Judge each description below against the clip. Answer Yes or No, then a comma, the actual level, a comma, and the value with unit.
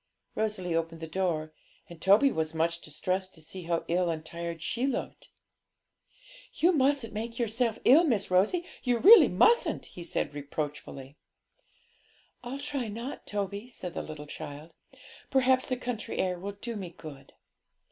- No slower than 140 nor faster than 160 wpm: Yes, average, 150 wpm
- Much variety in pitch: Yes, wide, 6.7 semitones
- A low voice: No, high, 190 Hz